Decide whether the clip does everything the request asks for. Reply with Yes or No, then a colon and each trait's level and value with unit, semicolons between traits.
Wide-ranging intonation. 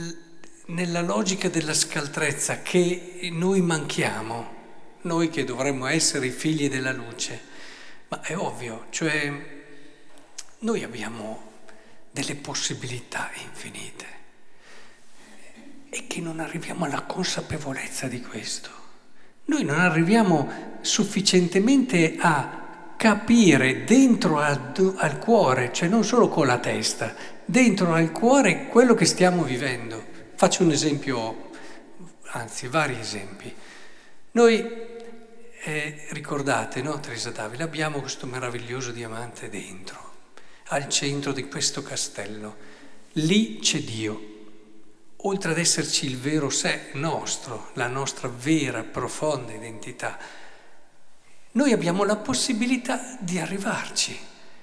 Yes: wide, 6.3 semitones